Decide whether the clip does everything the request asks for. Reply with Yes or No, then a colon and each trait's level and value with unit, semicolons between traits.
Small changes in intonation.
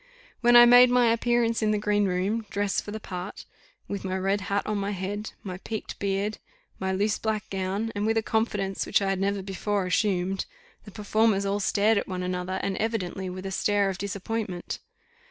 Yes: narrow, 2.2 semitones